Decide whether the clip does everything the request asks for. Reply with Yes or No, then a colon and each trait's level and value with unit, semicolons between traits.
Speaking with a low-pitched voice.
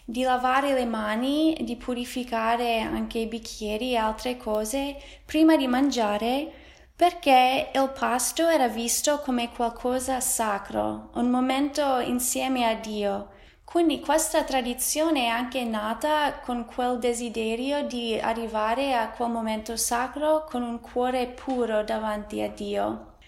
No: high, 245 Hz